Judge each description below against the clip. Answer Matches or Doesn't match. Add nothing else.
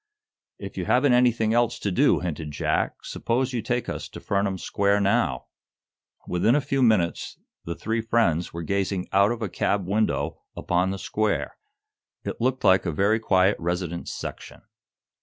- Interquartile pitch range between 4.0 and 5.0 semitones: Matches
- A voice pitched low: Matches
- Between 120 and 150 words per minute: Doesn't match